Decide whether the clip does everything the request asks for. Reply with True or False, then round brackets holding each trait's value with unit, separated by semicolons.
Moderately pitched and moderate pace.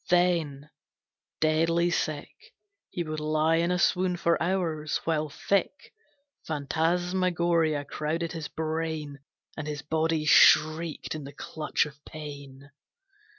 False (160 Hz; 115 wpm)